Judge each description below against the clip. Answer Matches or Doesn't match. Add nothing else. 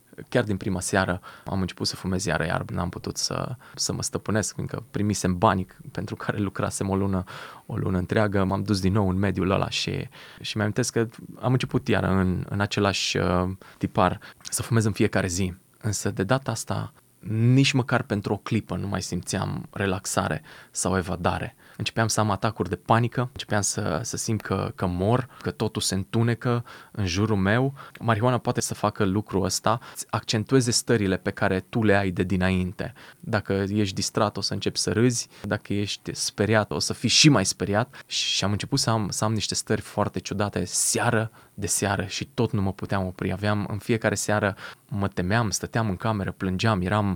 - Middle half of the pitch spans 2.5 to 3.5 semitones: Matches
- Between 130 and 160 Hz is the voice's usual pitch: Doesn't match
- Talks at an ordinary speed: Doesn't match